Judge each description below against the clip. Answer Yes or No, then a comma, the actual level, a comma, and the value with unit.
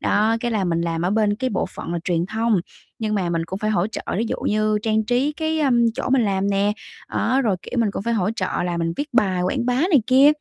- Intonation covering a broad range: No, average, 4.6 semitones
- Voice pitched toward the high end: Yes, high, 215 Hz